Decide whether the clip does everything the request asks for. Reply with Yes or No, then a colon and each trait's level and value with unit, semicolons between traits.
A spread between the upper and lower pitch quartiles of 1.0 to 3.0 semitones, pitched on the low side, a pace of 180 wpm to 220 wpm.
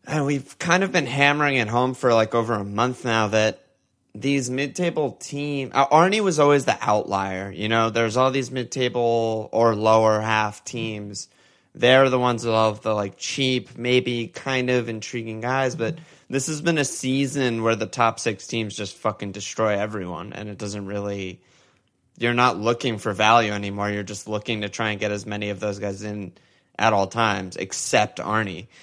No: average, 3.7 semitones; low, 115 Hz; average, 190 wpm